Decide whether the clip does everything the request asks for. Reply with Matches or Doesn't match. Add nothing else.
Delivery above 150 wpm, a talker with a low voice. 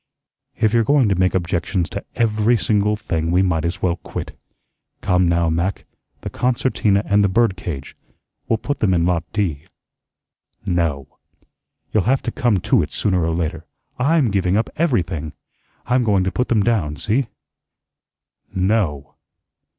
Matches